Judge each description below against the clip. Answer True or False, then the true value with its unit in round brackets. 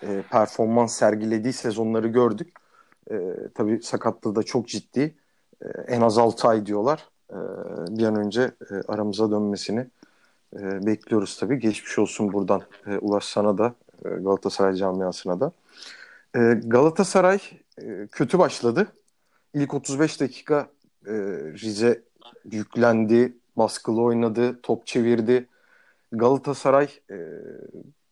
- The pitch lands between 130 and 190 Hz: False (115 Hz)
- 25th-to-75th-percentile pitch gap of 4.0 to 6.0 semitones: False (3.2 semitones)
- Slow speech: False (115 wpm)